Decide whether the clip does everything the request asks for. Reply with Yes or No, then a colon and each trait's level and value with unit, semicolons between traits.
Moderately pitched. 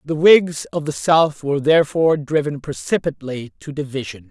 Yes: medium, 150 Hz